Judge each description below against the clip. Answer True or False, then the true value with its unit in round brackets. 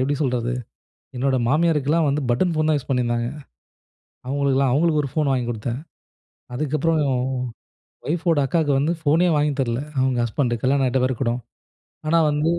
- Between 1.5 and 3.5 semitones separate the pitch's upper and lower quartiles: True (3.2 semitones)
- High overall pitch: False (140 Hz)